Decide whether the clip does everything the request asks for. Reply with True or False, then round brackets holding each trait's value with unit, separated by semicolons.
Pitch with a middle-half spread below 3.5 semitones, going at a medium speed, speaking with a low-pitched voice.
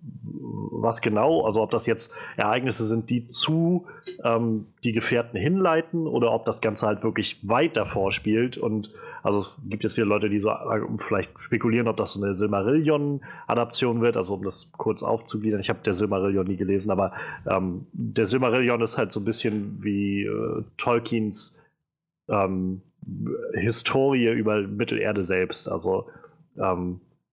True (2.9 semitones; 155 wpm; 110 Hz)